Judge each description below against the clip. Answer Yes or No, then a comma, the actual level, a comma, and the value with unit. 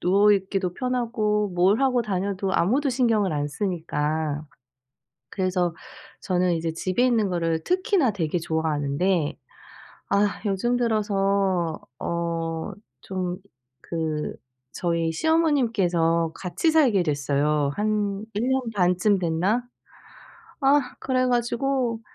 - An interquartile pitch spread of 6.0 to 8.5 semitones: No, wide, 5.5 semitones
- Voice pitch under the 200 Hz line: Yes, high, 190 Hz